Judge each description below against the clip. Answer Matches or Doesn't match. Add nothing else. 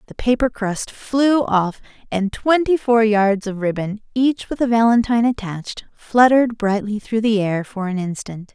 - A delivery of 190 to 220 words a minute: Doesn't match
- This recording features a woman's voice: Matches